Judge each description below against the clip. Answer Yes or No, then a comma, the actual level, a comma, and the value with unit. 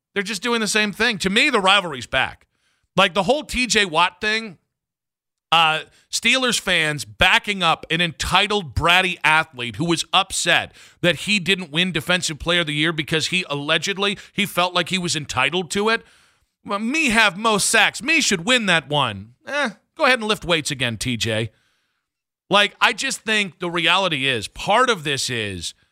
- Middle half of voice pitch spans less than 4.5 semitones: No, average, 5.3 semitones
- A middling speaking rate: Yes, average, 180 wpm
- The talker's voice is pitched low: No, medium, 180 Hz